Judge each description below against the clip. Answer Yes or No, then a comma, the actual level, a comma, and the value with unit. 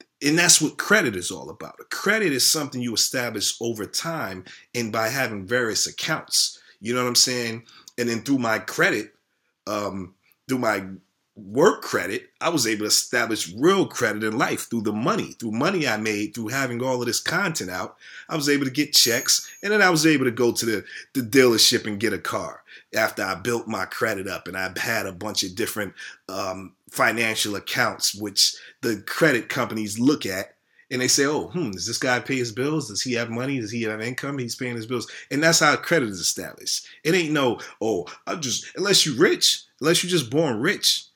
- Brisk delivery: Yes, fast, 210 wpm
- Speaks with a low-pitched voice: Yes, low, 120 Hz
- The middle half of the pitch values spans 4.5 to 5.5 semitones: No, average, 3.9 semitones